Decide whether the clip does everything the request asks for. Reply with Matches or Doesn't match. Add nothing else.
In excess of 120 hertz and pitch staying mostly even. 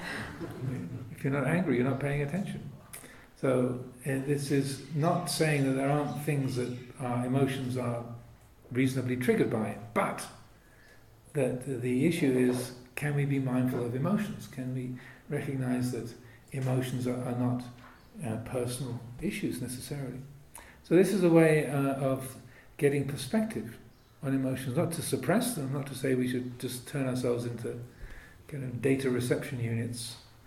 Matches